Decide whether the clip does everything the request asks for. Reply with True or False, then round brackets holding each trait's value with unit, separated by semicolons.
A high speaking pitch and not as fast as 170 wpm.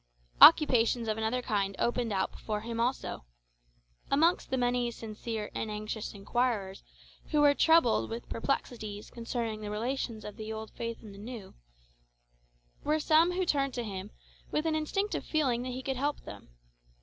True (235 Hz; 160 wpm)